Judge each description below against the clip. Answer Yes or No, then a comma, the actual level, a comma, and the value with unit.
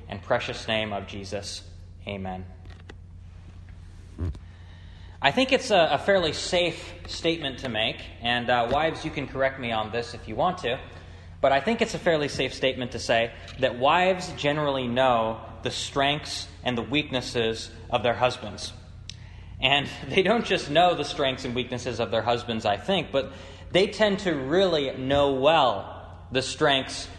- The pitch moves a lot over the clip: Yes, wide, 7.3 semitones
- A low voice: Yes, low, 120 Hz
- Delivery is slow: No, average, 165 wpm